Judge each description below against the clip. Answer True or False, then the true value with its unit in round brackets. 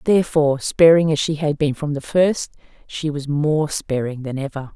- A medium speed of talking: True (190 wpm)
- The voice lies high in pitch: False (150 Hz)